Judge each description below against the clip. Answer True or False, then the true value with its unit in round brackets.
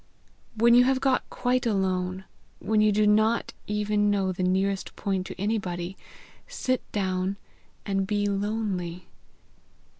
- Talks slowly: True (130 wpm)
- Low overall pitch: False (205 Hz)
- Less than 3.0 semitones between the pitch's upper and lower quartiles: True (2.4 semitones)